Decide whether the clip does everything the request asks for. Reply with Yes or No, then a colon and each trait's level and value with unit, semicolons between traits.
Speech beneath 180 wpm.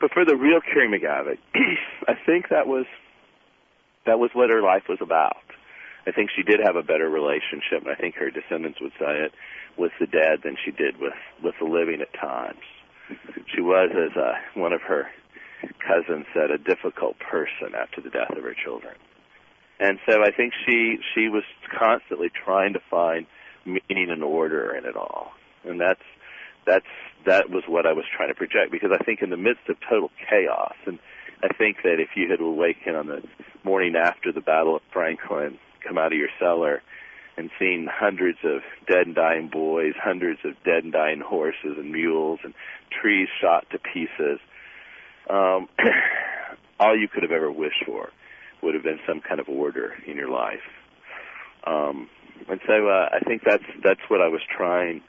No: average, 185 wpm